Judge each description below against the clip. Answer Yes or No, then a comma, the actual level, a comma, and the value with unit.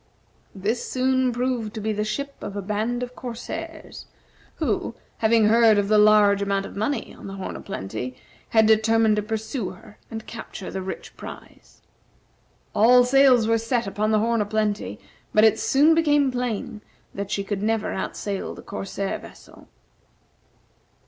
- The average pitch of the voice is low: No, high, 220 Hz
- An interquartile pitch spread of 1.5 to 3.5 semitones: Yes, average, 2.9 semitones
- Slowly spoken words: No, average, 165 wpm